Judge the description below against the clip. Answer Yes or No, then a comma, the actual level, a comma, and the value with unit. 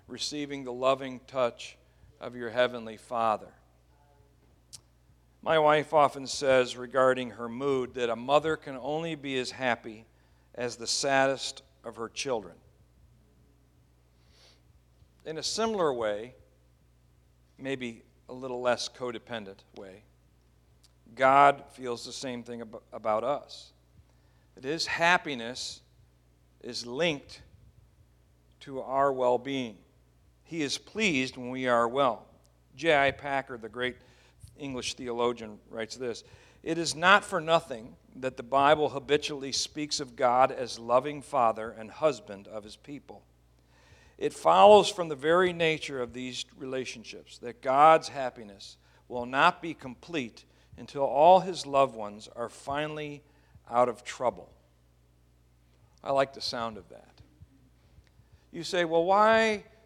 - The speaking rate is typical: No, slow, 125 wpm